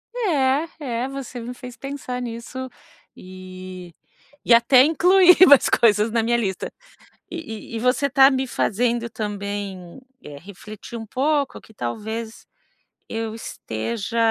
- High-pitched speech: Yes, high, 235 Hz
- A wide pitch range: No, average, 4.2 semitones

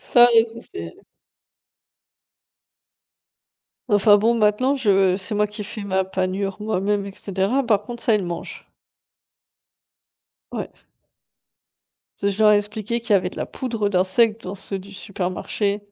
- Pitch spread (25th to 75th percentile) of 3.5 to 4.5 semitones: No, narrow, 2.5 semitones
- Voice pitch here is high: Yes, high, 205 Hz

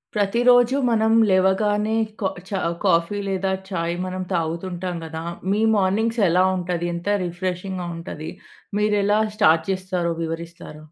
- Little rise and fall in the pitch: No, average, 3.2 semitones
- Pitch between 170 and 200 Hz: Yes, medium, 185 Hz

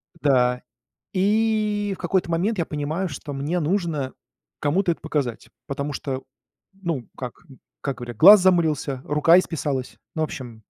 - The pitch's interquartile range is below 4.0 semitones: No, average, 5.2 semitones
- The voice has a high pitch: No, medium, 155 Hz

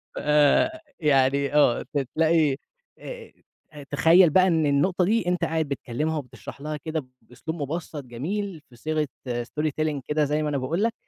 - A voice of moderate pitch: Yes, medium, 155 Hz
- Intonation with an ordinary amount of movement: Yes, average, 3.1 semitones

